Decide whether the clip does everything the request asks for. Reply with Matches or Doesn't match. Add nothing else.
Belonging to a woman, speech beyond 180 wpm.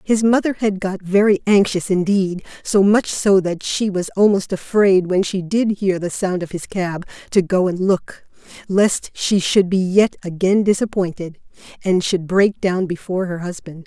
Doesn't match